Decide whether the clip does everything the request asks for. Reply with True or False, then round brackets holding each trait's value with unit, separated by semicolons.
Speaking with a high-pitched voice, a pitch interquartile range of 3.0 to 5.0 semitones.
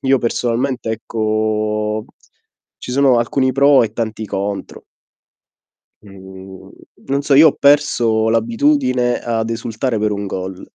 False (115 Hz; 3.5 semitones)